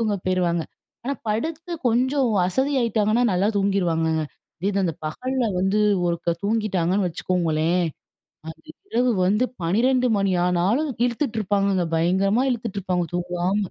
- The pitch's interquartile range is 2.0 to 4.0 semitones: No, average, 4.9 semitones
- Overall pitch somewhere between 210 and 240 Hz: No, high, 200 Hz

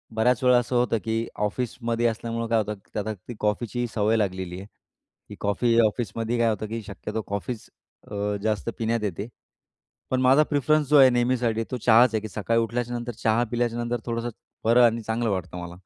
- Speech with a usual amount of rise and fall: No, narrow, 2.1 semitones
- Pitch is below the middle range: Yes, low, 115 Hz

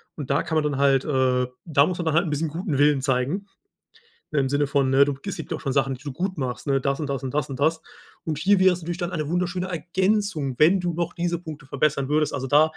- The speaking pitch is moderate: Yes, medium, 150 Hz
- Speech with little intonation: No, average, 3.9 semitones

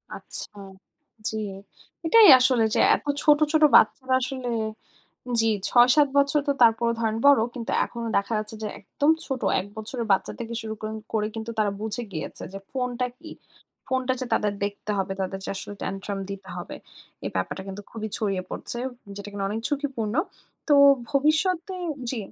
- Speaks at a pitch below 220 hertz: No, high, 230 Hz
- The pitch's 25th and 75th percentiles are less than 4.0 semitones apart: No, average, 4.3 semitones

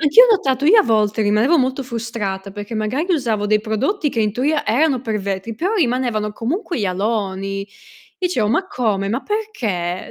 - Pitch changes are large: Yes, wide, 5.9 semitones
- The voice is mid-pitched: No, high, 230 Hz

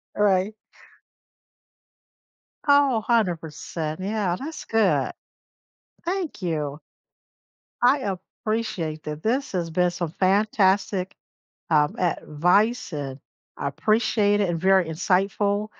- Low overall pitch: No, high, 190 Hz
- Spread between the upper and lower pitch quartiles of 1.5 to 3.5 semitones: No, average, 4.6 semitones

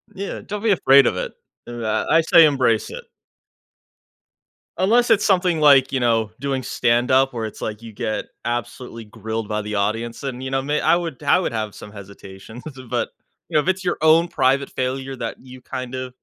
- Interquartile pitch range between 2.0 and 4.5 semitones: No, average, 5.0 semitones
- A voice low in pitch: Yes, low, 130 Hz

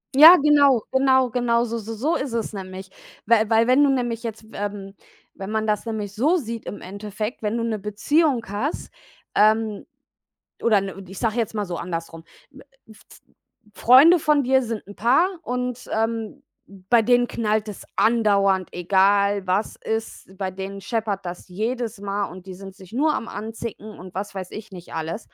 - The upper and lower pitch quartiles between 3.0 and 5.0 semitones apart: Yes, average, 3.5 semitones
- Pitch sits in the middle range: No, high, 220 Hz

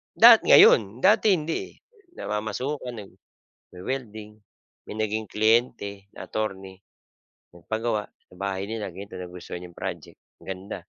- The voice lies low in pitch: Yes, low, 105 Hz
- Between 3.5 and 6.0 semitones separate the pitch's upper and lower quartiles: No, average, 3.1 semitones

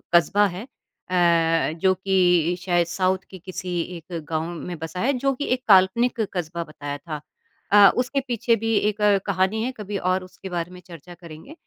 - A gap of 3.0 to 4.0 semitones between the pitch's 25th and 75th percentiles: Yes, average, 3.3 semitones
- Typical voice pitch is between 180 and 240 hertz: Yes, medium, 185 Hz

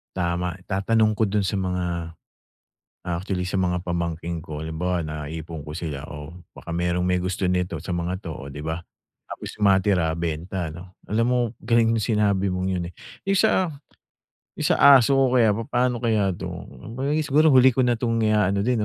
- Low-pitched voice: Yes, very low, 95 Hz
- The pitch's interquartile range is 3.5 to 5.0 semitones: Yes, average, 4.6 semitones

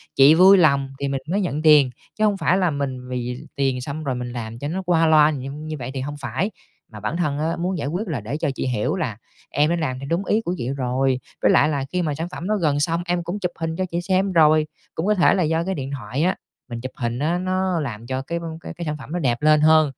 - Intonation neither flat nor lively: Yes, average, 4.6 semitones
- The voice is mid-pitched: Yes, medium, 150 Hz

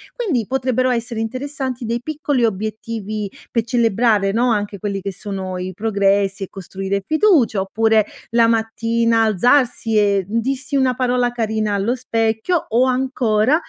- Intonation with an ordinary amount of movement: Yes, average, 3.5 semitones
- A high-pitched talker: Yes, high, 225 Hz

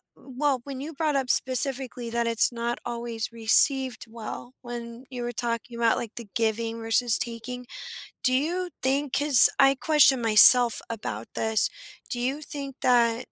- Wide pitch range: No, narrow, 2.5 semitones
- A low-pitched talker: No, high, 240 Hz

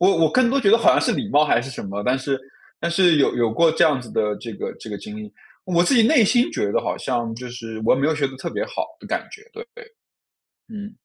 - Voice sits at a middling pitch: Yes, medium, 155 Hz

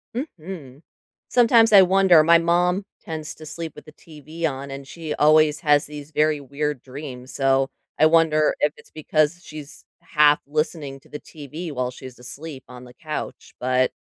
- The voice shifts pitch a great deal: No, average, 2.9 semitones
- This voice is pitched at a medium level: Yes, medium, 150 Hz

